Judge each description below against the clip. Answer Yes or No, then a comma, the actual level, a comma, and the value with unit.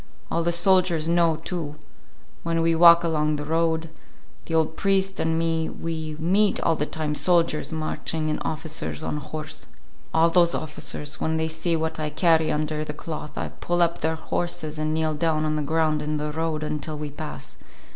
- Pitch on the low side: No, medium, 160 Hz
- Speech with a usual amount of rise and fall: No, narrow, 1.5 semitones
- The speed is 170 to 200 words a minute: Yes, average, 185 wpm